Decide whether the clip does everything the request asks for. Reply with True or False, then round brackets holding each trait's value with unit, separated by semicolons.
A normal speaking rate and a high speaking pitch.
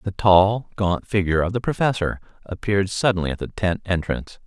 False (175 wpm; 95 Hz)